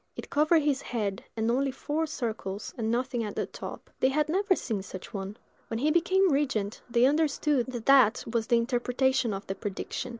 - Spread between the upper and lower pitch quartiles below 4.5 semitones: No, average, 4.9 semitones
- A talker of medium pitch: No, very high, 250 Hz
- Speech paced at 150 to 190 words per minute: No, average, 200 wpm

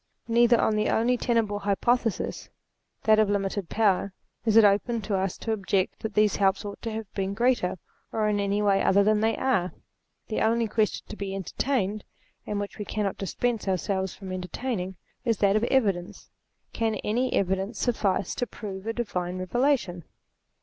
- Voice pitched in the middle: No, high, 210 Hz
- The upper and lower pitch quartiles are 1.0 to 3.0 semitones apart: Yes, narrow, 2.6 semitones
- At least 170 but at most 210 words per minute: Yes, average, 180 wpm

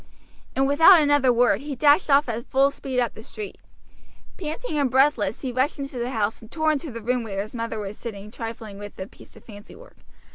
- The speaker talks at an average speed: No, fast, 220 wpm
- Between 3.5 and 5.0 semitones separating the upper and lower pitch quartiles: Yes, average, 4.5 semitones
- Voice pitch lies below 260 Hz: Yes, very high, 250 Hz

